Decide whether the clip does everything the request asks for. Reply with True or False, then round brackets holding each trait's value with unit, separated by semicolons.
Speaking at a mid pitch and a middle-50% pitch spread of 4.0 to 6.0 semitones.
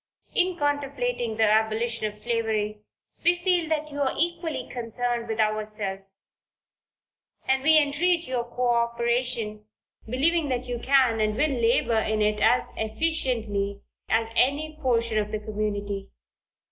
False (235 Hz; 4.9 semitones)